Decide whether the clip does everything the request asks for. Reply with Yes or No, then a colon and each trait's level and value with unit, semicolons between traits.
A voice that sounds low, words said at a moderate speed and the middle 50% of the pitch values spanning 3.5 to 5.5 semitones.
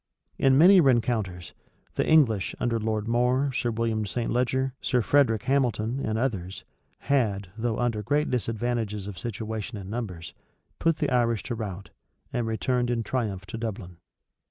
No: low, 115 Hz; average, 155 wpm; average, 2.9 semitones